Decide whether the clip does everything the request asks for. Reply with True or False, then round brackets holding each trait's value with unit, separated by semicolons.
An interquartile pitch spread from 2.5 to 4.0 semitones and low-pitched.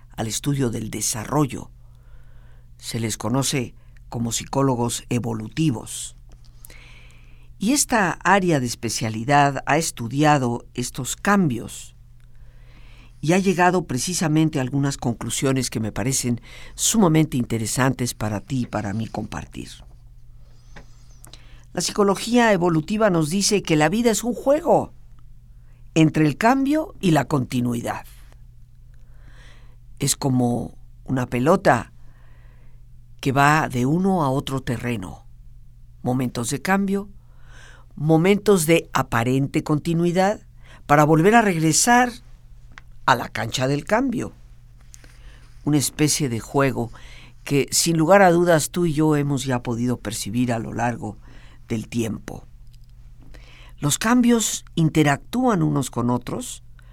False (4.6 semitones; 125 Hz)